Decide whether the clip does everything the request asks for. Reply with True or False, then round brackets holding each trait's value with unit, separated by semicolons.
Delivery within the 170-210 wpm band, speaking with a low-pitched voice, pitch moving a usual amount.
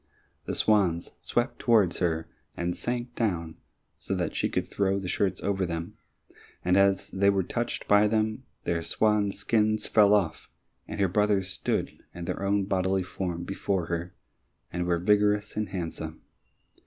False (160 wpm; 95 Hz; 3.0 semitones)